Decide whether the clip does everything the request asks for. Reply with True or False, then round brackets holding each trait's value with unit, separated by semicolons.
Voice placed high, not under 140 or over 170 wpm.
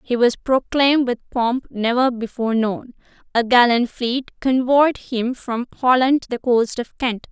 True (245 Hz; 165 wpm)